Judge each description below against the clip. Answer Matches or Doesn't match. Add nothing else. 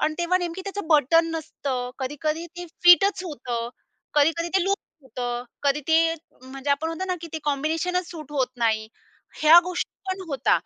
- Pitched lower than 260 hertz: Doesn't match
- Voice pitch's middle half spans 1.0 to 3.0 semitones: Doesn't match